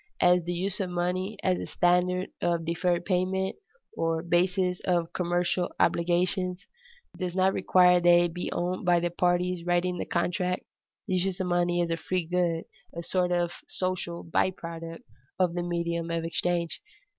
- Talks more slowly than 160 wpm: No, average, 170 wpm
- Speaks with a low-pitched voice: No, medium, 175 Hz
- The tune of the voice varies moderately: No, narrow, 1.0 semitones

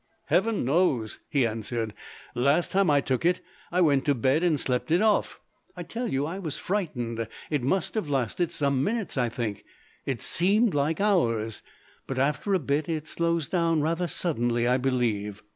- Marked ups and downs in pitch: Yes, wide, 6.2 semitones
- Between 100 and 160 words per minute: No, average, 175 wpm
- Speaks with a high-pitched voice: No, medium, 145 Hz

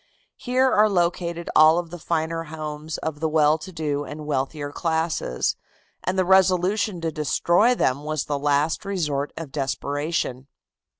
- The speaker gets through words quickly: No, average, 155 wpm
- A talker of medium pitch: Yes, medium, 160 Hz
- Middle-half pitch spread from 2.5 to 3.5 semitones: Yes, average, 2.9 semitones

